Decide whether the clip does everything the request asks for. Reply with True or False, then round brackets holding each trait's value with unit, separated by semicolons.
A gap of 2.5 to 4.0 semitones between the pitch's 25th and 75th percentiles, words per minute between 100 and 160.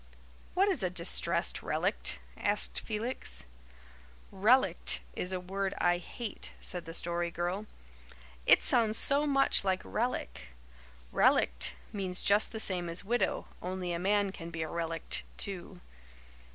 True (3.7 semitones; 140 wpm)